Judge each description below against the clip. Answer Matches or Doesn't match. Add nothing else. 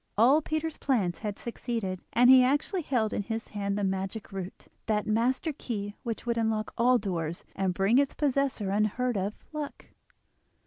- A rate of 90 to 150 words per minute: Doesn't match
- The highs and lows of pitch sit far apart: Doesn't match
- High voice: Matches